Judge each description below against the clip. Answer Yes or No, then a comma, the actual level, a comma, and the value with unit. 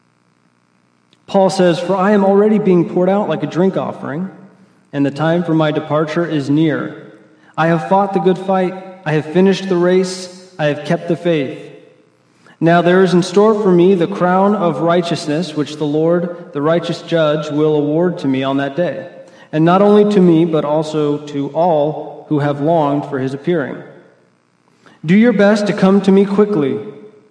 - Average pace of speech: Yes, average, 185 wpm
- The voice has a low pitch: No, medium, 170 Hz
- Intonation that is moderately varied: Yes, average, 3.7 semitones